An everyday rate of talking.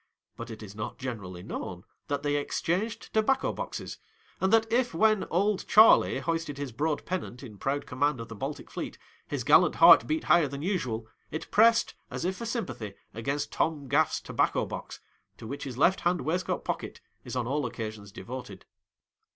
Yes: average, 180 wpm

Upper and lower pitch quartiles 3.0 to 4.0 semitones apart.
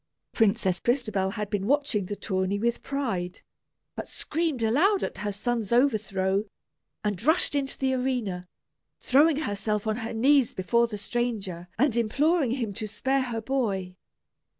No: average, 4.7 semitones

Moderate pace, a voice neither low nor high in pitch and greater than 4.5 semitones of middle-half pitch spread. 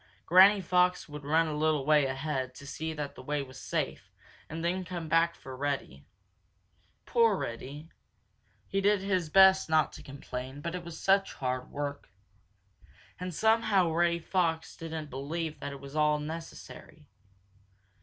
No: average, 160 wpm; medium, 160 Hz; average, 3.9 semitones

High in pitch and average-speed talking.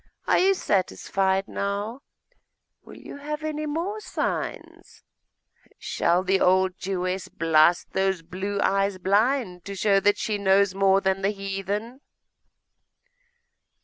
No: high, 195 Hz; slow, 120 wpm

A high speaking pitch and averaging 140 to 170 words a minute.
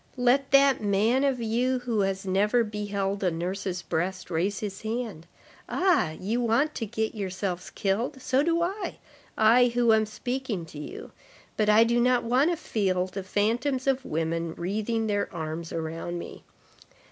Yes: high, 215 Hz; average, 160 wpm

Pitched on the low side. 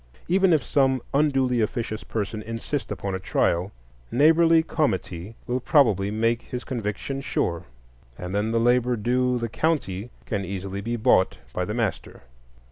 Yes: low, 115 Hz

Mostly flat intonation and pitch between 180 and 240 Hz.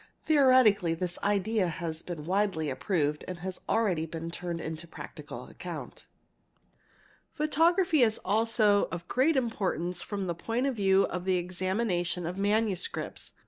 No: average, 4.6 semitones; high, 190 Hz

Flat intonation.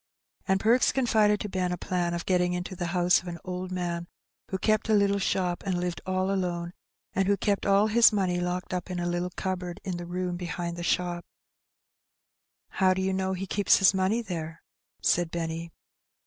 Yes: narrow, 1.7 semitones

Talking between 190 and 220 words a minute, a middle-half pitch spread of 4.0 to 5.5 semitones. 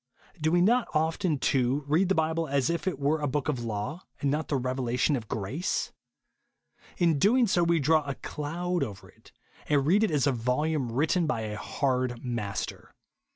Yes: average, 195 wpm; average, 4.3 semitones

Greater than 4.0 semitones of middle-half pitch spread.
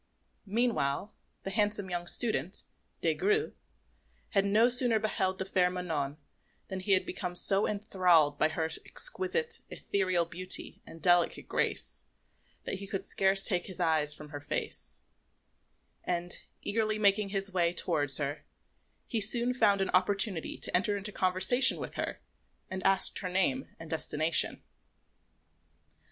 No: average, 3.4 semitones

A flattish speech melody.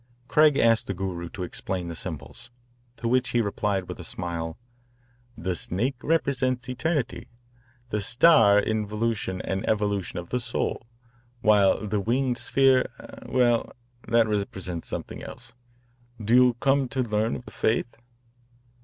No: average, 4.5 semitones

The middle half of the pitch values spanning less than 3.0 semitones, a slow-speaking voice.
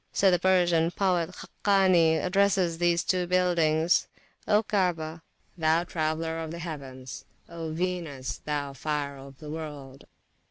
Yes: narrow, 2.6 semitones; slow, 130 wpm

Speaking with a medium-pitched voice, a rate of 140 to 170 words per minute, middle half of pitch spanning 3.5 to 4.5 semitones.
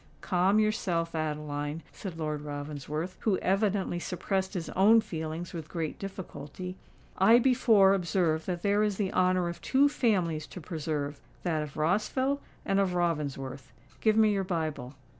Yes: medium, 175 Hz; average, 145 wpm; average, 4.1 semitones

